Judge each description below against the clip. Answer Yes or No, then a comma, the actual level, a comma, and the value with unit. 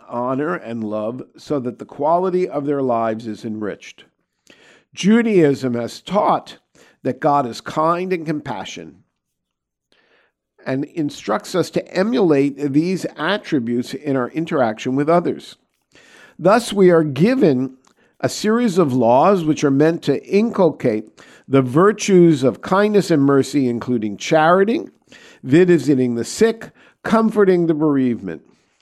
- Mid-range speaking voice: Yes, medium, 150 Hz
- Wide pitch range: Yes, wide, 6.6 semitones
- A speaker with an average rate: No, slow, 125 wpm